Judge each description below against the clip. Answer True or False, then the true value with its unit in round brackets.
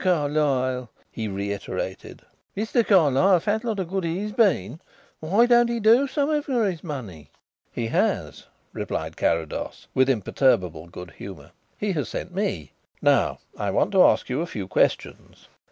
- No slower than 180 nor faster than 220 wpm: False (155 wpm)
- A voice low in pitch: False (160 Hz)